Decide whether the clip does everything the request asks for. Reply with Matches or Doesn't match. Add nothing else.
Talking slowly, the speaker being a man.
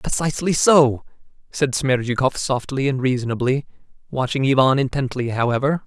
Matches